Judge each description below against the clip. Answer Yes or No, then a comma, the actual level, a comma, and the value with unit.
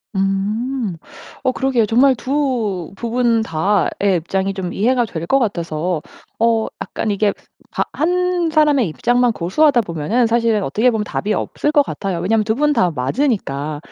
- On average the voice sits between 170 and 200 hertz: No, high, 220 Hz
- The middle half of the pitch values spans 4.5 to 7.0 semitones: Yes, average, 5.1 semitones